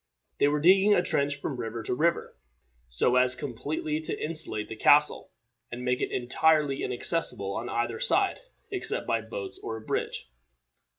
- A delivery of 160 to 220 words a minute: Yes, average, 165 wpm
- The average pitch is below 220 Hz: Yes, medium, 140 Hz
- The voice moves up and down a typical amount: Yes, average, 5.0 semitones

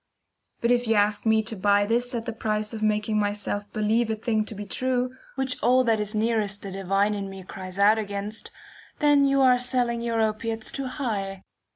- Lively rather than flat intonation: No, narrow, 2.6 semitones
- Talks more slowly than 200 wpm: No, fast, 205 wpm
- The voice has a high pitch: Yes, high, 220 Hz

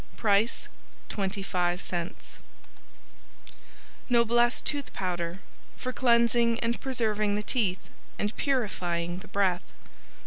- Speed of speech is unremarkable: No, slow, 90 wpm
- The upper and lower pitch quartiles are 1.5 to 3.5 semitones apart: No, average, 4.4 semitones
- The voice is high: Yes, high, 210 Hz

